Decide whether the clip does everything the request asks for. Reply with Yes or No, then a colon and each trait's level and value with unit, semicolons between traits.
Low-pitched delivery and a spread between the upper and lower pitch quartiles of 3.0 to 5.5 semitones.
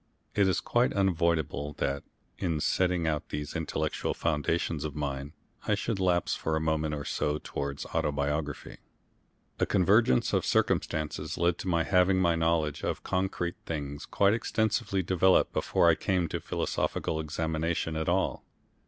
Yes: very low, 80 Hz; average, 3.5 semitones